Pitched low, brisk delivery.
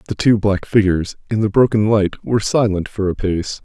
Yes: low, 100 Hz; fast, 215 wpm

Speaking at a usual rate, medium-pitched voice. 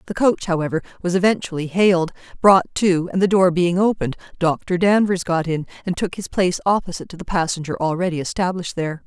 Yes: average, 185 wpm; medium, 175 Hz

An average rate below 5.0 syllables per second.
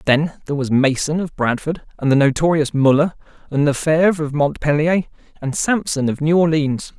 No: 5.3 syllables/s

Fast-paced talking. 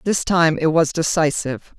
No: average, 170 wpm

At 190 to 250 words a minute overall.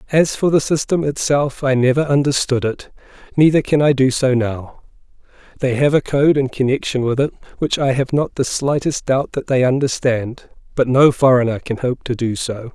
Yes: average, 195 wpm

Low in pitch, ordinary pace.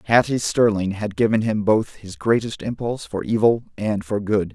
Yes: low, 110 Hz; average, 185 wpm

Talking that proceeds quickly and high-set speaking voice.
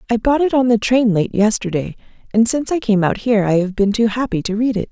Yes: fast, 270 wpm; high, 220 Hz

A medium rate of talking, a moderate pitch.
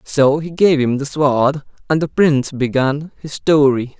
Yes: average, 180 wpm; medium, 145 Hz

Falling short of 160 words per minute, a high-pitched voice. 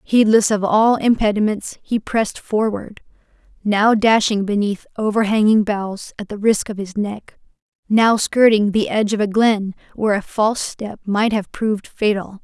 Yes: average, 150 wpm; high, 210 Hz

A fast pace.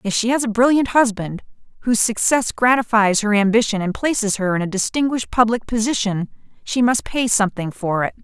No: average, 180 wpm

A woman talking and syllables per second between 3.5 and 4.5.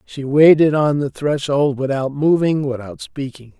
No: male; 4.3 syllables/s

